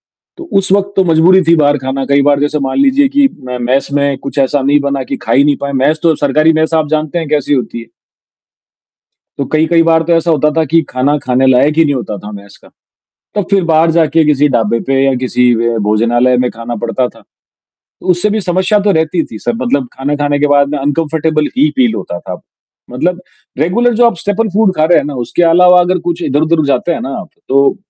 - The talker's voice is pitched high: No, medium, 150 Hz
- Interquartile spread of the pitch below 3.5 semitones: No, average, 4.0 semitones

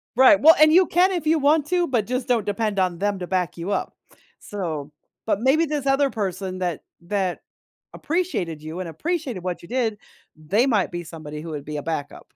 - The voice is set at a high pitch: Yes, high, 205 Hz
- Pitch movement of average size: No, wide, 8.4 semitones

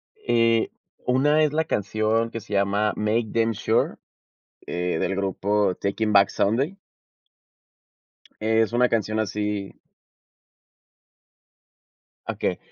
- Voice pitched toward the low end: Yes, low, 110 Hz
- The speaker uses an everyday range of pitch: No, narrow, 2.3 semitones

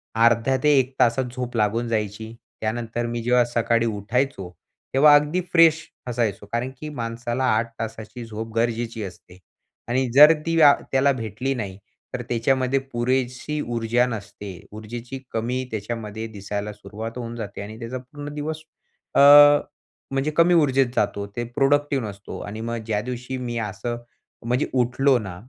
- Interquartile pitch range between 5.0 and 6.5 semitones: No, average, 3.1 semitones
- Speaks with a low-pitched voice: Yes, low, 120 Hz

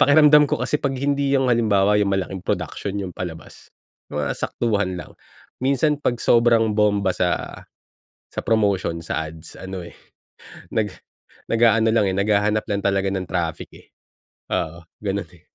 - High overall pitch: No, low, 100 Hz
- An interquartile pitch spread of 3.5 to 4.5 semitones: Yes, average, 4.2 semitones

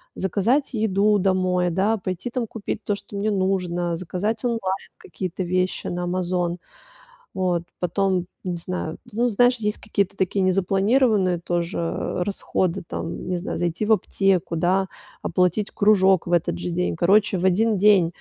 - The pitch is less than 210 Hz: Yes, high, 190 Hz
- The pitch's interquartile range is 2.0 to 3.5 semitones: Yes, narrow, 2.6 semitones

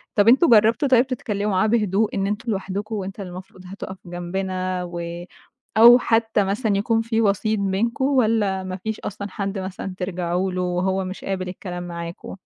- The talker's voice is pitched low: No, high, 195 Hz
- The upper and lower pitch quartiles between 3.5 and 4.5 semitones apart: No, average, 3.0 semitones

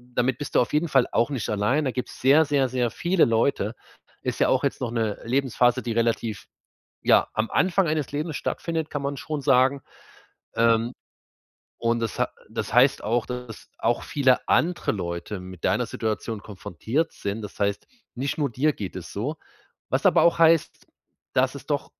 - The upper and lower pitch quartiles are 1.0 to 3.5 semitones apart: No, average, 4.5 semitones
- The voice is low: Yes, low, 125 Hz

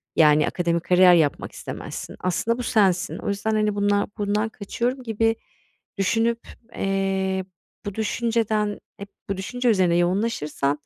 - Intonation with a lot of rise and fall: No, average, 3.4 semitones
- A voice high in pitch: Yes, high, 200 Hz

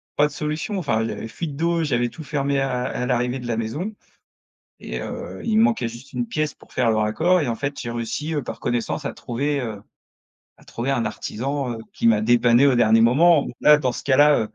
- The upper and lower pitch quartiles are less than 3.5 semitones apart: No, average, 4.1 semitones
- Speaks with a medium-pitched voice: No, low, 130 Hz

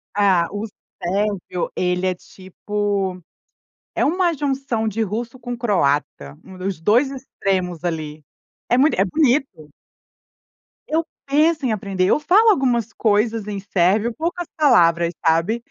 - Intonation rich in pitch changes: Yes, wide, 6.1 semitones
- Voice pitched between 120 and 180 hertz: No, high, 210 Hz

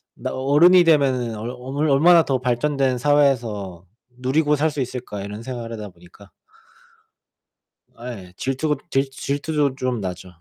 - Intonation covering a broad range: No, average, 4.0 semitones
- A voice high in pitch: No, low, 130 Hz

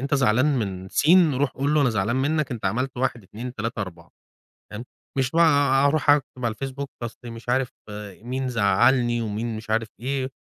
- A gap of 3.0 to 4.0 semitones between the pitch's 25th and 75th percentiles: Yes, average, 3.3 semitones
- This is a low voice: Yes, low, 125 Hz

